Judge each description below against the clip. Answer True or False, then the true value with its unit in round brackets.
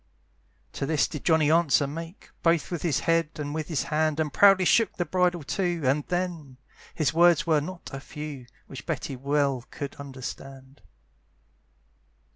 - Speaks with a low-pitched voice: False (155 Hz)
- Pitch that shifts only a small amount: False (3.4 semitones)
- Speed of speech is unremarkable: True (160 wpm)